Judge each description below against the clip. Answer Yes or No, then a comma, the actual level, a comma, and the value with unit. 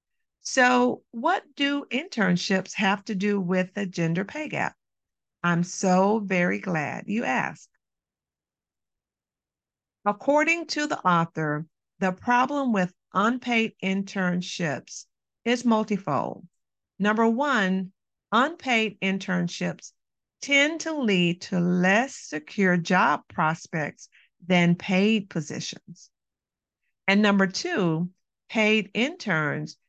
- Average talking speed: No, slow, 100 wpm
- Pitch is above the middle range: Yes, high, 195 Hz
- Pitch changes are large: No, average, 4.6 semitones